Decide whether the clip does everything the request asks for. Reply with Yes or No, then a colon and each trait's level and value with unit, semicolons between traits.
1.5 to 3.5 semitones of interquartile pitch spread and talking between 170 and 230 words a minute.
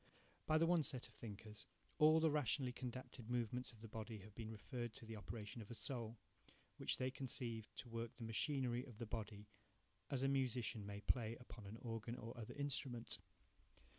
Yes: narrow, 2.6 semitones; average, 190 wpm